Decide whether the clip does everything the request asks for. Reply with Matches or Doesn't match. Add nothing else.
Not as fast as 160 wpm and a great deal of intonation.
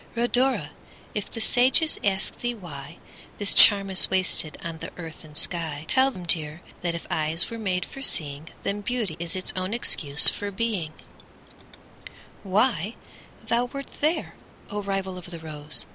Matches